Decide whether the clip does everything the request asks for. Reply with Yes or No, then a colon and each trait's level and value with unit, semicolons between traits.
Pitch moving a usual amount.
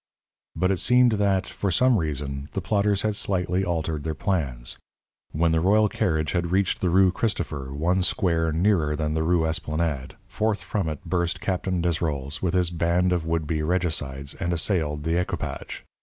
Yes: average, 3.3 semitones